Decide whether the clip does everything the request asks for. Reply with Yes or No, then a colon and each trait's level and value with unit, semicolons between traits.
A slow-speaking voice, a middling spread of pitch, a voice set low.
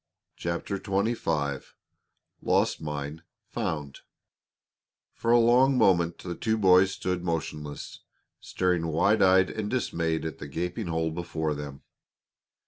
Yes: slow, 120 wpm; average, 3.9 semitones; very low, 85 Hz